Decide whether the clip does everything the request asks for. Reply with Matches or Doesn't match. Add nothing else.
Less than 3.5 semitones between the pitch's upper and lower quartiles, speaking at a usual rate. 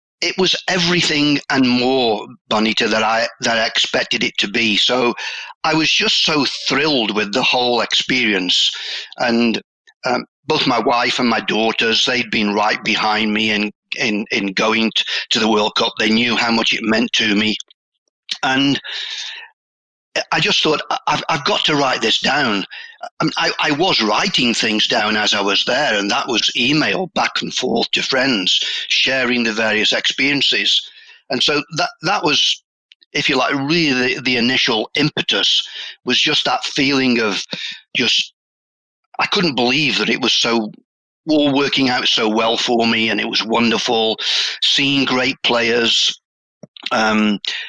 Doesn't match